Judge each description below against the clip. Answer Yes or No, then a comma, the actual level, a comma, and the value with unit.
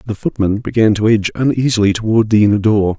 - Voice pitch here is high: No, low, 110 Hz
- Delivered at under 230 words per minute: Yes, average, 200 wpm